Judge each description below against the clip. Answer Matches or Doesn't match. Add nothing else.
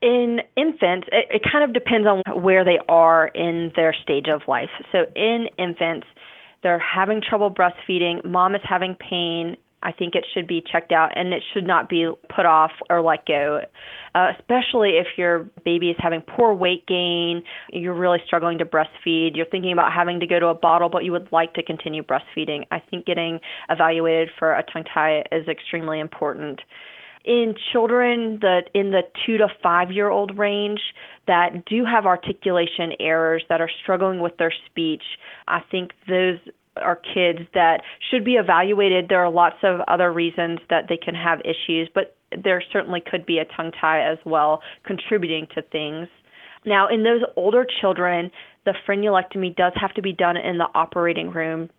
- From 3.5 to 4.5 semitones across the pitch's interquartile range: Doesn't match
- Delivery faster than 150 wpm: Matches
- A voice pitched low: Doesn't match